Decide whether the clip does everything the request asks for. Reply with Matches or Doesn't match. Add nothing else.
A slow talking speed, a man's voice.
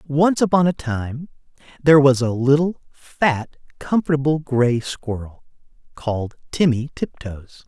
Matches